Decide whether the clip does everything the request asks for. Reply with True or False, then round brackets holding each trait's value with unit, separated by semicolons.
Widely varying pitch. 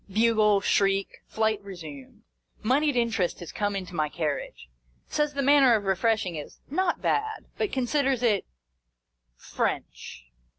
True (5.9 semitones)